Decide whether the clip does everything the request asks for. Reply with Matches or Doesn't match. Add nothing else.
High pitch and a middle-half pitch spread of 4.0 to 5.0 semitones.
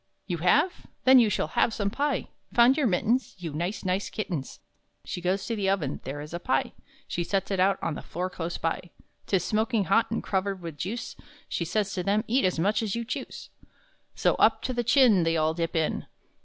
Matches